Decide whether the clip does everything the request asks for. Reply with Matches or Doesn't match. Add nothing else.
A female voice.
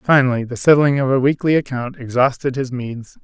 Doesn't match